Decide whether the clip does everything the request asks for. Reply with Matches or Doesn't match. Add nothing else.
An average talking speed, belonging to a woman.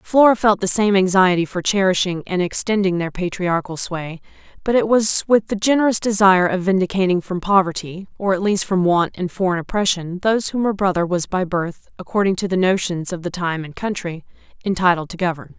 Matches